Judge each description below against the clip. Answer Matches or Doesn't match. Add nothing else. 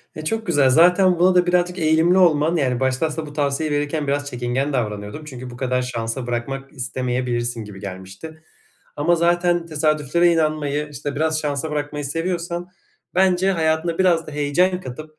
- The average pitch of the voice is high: Doesn't match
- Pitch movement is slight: Doesn't match